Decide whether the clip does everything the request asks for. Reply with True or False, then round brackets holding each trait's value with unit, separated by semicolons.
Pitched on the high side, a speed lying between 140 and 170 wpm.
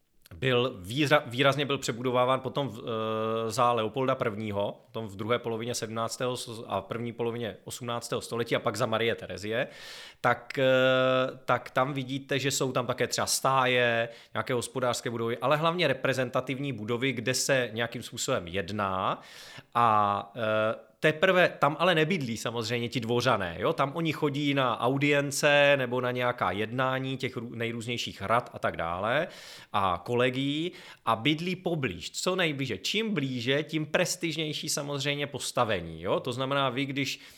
False (125 Hz; 150 wpm)